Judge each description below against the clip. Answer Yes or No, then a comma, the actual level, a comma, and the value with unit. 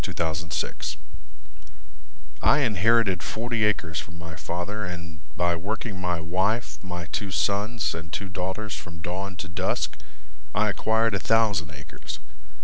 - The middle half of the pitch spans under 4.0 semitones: No, average, 4.3 semitones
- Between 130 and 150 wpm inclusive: Yes, average, 140 wpm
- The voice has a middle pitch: No, very low, 95 Hz